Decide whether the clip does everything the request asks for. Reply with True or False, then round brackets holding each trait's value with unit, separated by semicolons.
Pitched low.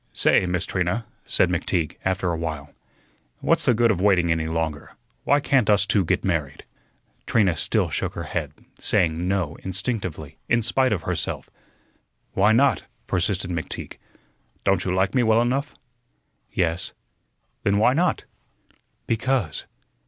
True (95 Hz)